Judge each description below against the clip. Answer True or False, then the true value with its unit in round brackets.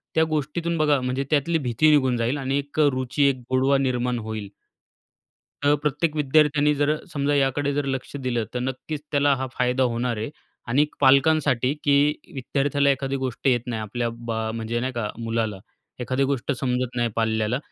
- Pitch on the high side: False (135 Hz)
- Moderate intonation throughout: True (3.0 semitones)